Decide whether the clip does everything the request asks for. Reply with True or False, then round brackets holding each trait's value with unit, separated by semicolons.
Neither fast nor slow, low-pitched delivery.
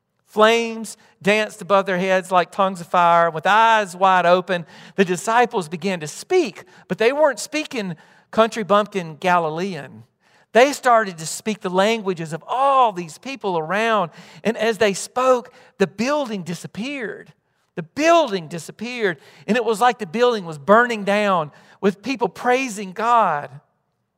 False (145 wpm; 205 Hz)